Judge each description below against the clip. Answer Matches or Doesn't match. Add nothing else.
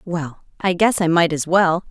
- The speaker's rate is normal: Doesn't match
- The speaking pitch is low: Doesn't match